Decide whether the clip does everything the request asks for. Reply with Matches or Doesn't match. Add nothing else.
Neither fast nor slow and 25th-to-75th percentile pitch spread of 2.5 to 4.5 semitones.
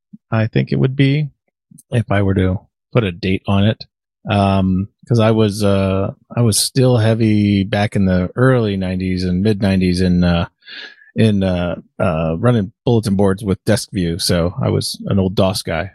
Matches